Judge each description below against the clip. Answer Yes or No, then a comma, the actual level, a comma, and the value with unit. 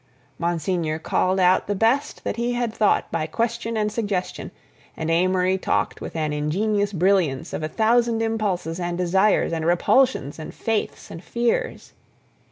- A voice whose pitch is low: No, high, 190 Hz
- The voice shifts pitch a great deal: No, average, 5.0 semitones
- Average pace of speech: Yes, average, 155 wpm